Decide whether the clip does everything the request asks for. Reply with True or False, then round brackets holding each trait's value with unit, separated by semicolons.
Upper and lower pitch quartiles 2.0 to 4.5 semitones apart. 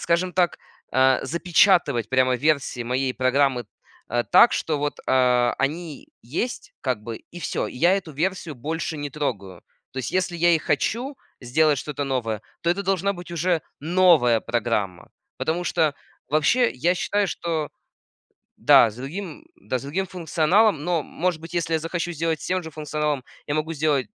False (5.0 semitones)